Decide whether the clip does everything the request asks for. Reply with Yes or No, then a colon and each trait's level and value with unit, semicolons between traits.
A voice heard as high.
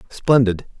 No: low, 115 Hz